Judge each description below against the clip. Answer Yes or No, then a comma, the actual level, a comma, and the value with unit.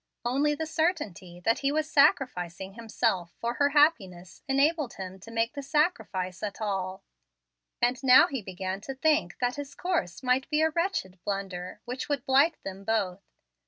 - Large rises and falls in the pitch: Yes, wide, 7.2 semitones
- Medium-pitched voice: No, high, 240 Hz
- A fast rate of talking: No, average, 165 wpm